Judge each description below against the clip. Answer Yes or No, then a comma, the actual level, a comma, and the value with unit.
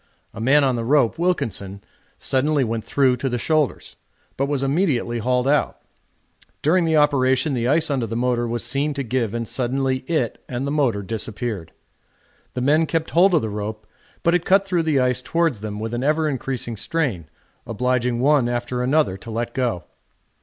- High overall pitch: No, low, 130 Hz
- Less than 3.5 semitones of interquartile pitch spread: No, average, 4.1 semitones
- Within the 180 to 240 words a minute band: Yes, average, 185 wpm